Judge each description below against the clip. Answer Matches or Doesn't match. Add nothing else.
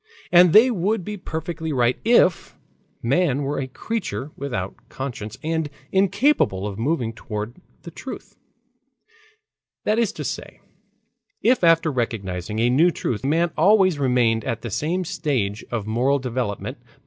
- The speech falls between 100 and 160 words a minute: Matches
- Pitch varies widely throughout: Matches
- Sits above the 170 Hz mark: Doesn't match